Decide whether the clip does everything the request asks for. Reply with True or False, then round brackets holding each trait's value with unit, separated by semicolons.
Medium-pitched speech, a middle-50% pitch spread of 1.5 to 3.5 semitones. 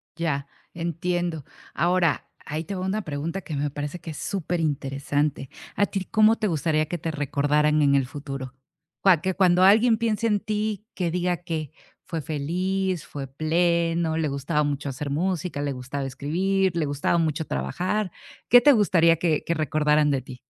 False (160 Hz; 4.1 semitones)